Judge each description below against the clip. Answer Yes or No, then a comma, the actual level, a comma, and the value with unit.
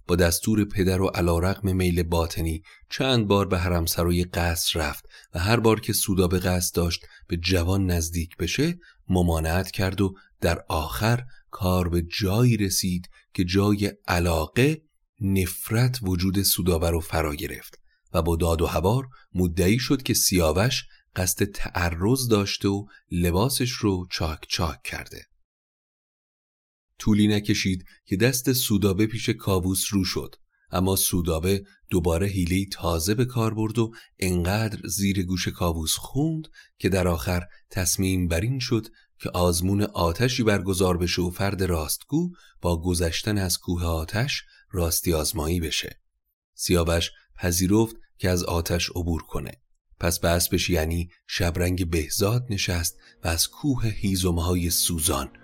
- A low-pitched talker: Yes, very low, 95 Hz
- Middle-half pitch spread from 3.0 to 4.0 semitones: Yes, average, 3.4 semitones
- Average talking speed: Yes, average, 135 wpm